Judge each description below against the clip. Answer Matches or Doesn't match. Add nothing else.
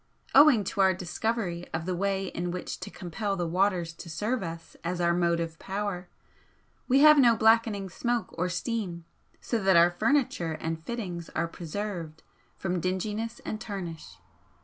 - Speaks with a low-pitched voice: Doesn't match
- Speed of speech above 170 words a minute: Doesn't match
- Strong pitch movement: Doesn't match